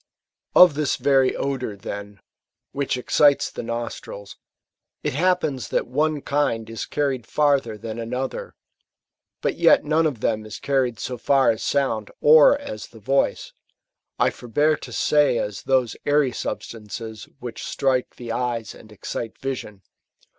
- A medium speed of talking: Yes, average, 150 wpm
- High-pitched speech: No, low, 130 Hz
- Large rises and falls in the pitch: No, average, 4.3 semitones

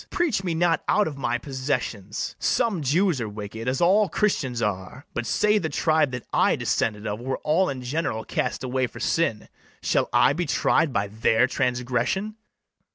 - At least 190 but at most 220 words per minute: No, average, 175 wpm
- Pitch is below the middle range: Yes, low, 130 Hz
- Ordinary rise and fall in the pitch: No, wide, 6.3 semitones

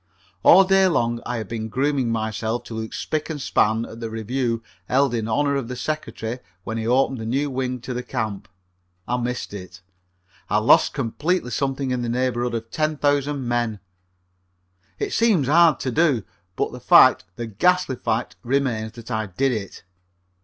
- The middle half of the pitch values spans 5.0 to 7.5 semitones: No, average, 3.7 semitones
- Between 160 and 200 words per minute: Yes, average, 180 wpm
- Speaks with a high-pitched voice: No, low, 125 Hz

